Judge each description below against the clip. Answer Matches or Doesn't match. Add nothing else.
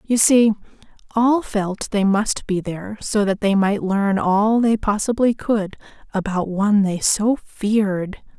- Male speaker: Doesn't match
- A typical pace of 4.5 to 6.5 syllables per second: Doesn't match